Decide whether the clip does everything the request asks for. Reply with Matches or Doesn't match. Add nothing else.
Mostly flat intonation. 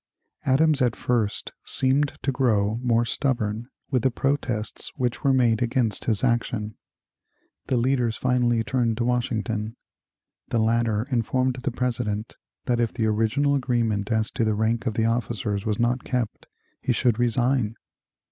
Matches